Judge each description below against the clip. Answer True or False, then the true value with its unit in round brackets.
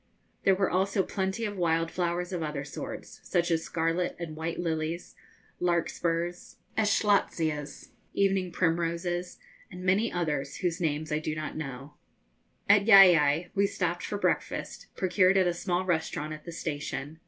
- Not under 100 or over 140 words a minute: False (150 wpm)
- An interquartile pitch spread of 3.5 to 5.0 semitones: False (2.8 semitones)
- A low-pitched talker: False (170 Hz)